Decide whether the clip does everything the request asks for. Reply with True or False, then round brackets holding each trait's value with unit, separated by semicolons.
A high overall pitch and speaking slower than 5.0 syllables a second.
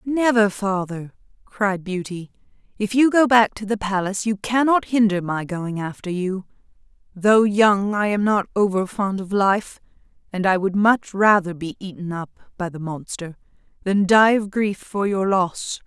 True (200 Hz; 4.4 syllables/s)